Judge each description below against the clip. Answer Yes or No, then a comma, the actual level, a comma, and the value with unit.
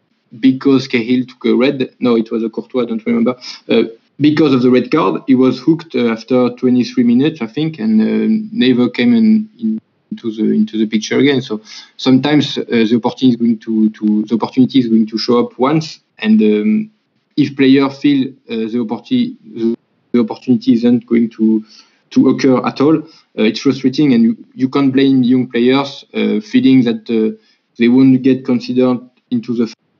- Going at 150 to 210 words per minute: Yes, average, 190 wpm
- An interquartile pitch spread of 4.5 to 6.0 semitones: Yes, average, 5.3 semitones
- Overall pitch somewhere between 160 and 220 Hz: No, low, 130 Hz